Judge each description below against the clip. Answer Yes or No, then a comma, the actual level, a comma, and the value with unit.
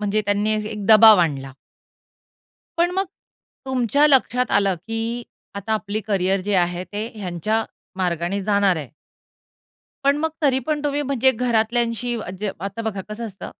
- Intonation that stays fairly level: No, average, 3.8 semitones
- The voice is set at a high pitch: Yes, high, 215 Hz